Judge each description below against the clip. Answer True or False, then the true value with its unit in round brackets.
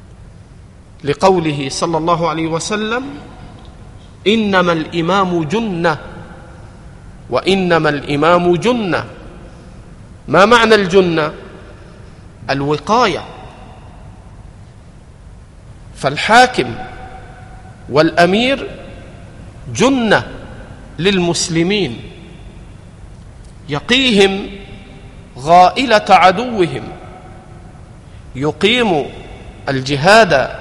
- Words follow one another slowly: True (45 wpm)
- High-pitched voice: False (160 Hz)